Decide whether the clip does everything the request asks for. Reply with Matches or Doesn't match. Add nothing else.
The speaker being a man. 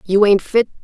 Doesn't match